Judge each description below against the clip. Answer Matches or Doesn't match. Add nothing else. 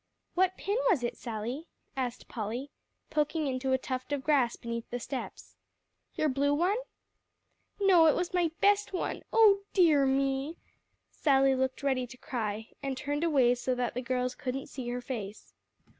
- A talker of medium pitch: Doesn't match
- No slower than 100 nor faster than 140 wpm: Doesn't match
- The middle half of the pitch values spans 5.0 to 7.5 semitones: Doesn't match